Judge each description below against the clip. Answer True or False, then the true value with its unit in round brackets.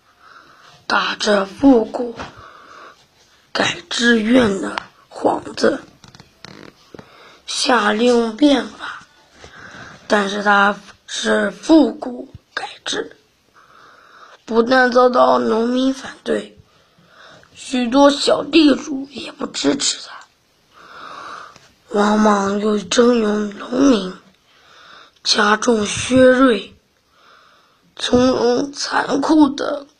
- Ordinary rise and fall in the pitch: True (4.1 semitones)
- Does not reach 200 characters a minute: True (110 characters per minute)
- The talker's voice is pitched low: False (245 Hz)